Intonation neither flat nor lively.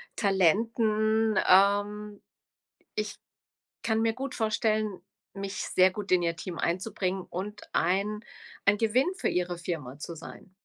Yes: average, 3.0 semitones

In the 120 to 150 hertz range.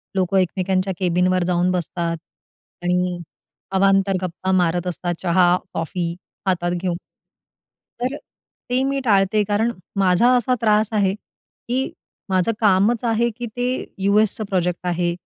No: high, 190 Hz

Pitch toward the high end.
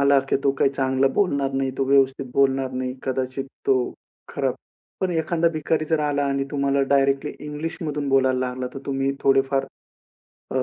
No: low, 135 Hz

